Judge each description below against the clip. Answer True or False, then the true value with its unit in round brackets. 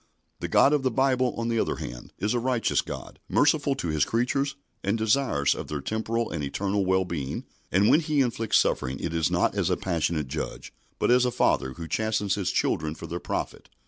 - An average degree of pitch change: False (7.1 semitones)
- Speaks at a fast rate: True (210 wpm)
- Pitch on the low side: True (105 Hz)